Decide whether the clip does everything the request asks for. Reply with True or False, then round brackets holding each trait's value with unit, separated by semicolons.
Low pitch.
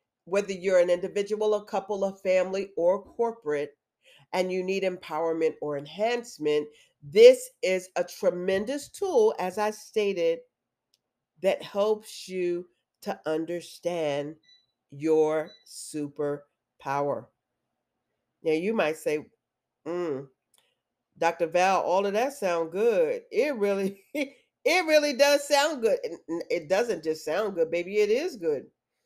False (185 Hz)